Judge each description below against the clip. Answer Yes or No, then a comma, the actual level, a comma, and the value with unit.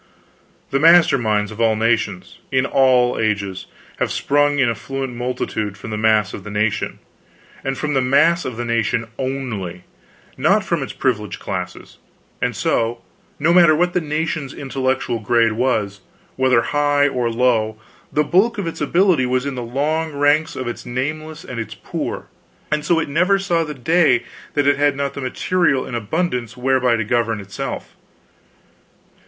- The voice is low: Yes, low, 130 Hz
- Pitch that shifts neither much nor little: Yes, average, 4.7 semitones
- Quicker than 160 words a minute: Yes, average, 170 wpm